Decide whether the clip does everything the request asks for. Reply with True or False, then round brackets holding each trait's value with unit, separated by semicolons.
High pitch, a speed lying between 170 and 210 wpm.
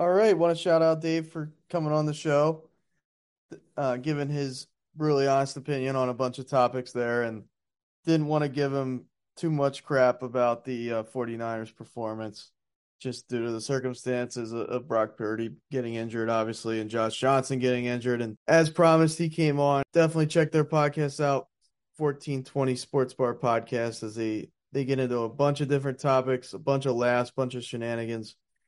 False (130 Hz; 185 wpm)